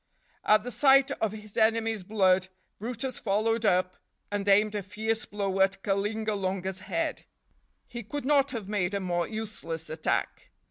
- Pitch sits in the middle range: No, high, 210 Hz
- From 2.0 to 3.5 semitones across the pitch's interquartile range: Yes, average, 2.8 semitones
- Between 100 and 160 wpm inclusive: Yes, average, 150 wpm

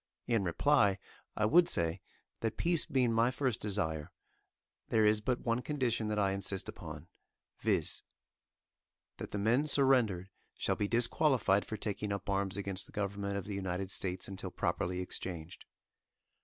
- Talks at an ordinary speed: Yes, average, 155 wpm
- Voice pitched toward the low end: Yes, low, 105 Hz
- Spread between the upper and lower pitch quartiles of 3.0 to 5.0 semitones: Yes, average, 3.6 semitones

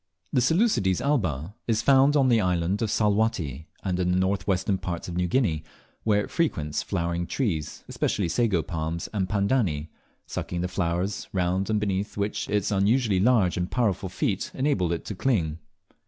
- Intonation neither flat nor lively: Yes, average, 4.2 semitones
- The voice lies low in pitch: Yes, very low, 95 Hz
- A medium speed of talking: Yes, average, 170 wpm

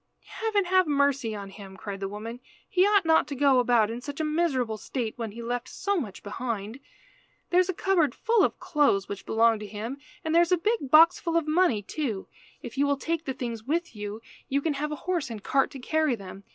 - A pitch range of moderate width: No, wide, 6.9 semitones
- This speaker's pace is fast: Yes, fast, 230 wpm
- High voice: Yes, very high, 275 Hz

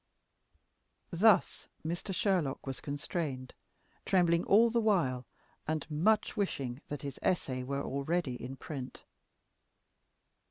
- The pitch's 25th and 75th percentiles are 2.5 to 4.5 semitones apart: No, wide, 5.6 semitones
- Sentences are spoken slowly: Yes, slow, 110 wpm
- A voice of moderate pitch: Yes, medium, 155 Hz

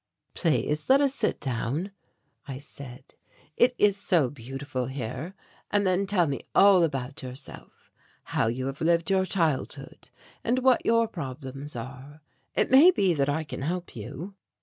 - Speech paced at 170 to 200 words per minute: No, average, 155 wpm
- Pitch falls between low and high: Yes, medium, 150 Hz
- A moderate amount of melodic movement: No, wide, 6.5 semitones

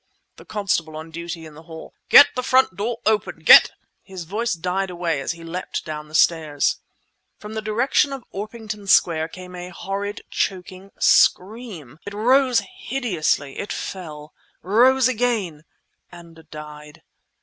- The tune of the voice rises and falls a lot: No, average, 5.0 semitones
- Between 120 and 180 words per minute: Yes, average, 140 wpm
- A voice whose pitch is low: No, medium, 185 Hz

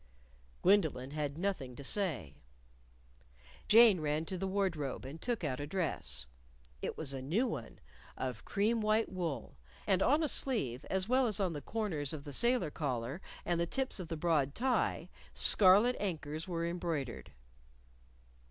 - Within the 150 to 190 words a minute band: Yes, average, 160 wpm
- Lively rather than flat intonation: Yes, wide, 6.1 semitones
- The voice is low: No, medium, 170 Hz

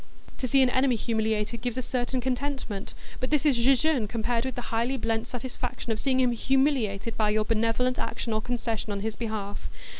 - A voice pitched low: No, high, 240 Hz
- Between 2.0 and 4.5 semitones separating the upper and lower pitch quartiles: Yes, average, 2.8 semitones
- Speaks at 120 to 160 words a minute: No, average, 190 wpm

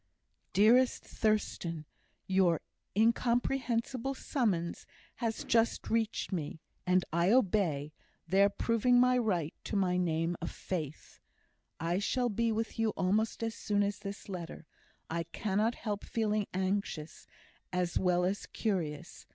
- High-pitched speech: Yes, high, 200 Hz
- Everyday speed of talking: No, slow, 125 wpm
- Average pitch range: Yes, average, 4.4 semitones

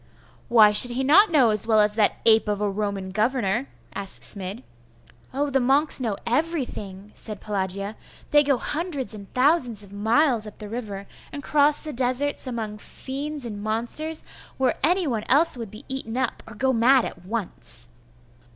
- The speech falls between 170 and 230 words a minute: Yes, average, 175 wpm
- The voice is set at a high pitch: Yes, high, 235 Hz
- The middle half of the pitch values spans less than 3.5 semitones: No, average, 4.7 semitones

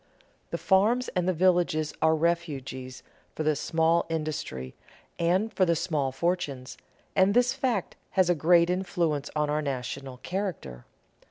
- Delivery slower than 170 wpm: Yes, average, 145 wpm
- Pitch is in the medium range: Yes, medium, 165 Hz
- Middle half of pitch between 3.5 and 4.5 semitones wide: Yes, average, 4.1 semitones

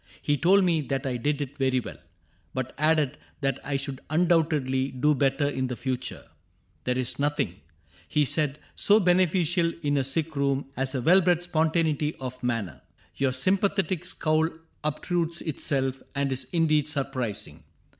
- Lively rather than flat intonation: No, average, 3.7 semitones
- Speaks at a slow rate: No, average, 165 wpm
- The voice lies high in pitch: No, medium, 145 Hz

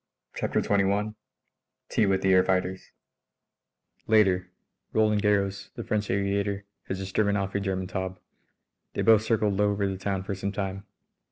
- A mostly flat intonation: Yes, narrow, 1.3 semitones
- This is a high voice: No, low, 100 Hz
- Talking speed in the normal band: Yes, average, 160 wpm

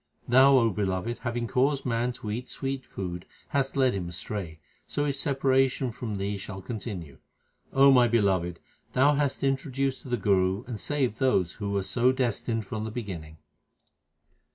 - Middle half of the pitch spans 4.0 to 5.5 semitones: Yes, average, 5.2 semitones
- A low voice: Yes, low, 120 Hz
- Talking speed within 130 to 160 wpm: No, average, 170 wpm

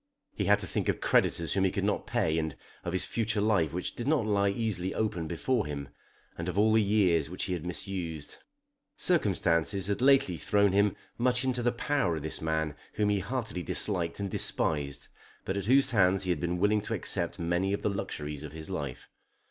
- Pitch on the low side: Yes, very low, 95 Hz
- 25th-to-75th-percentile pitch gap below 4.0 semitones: No, average, 4.3 semitones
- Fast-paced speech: Yes, fast, 210 wpm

